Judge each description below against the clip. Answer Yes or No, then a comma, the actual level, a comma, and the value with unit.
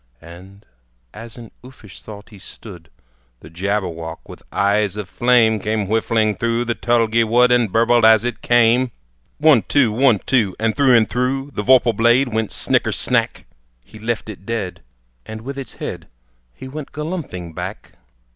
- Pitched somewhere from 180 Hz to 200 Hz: No, low, 115 Hz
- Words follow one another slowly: No, average, 165 wpm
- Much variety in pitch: No, average, 3.0 semitones